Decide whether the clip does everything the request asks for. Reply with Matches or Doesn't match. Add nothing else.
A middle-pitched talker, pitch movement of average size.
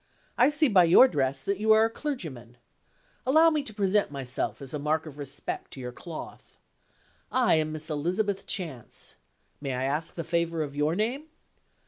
Doesn't match